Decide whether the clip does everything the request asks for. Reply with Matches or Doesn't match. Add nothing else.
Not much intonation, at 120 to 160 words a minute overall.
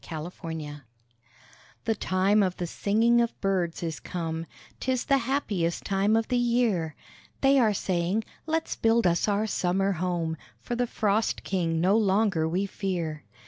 Doesn't match